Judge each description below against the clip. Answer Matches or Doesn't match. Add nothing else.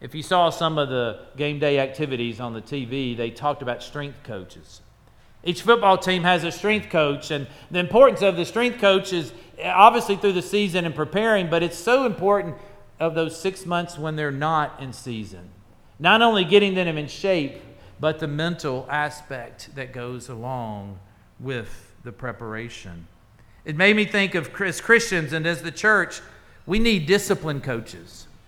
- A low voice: Doesn't match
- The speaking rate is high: Doesn't match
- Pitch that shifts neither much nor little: Doesn't match